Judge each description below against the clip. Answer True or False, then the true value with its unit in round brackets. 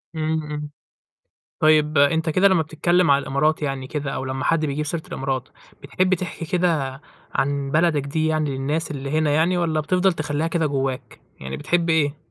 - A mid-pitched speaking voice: True (155 Hz)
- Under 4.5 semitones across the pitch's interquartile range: True (2.6 semitones)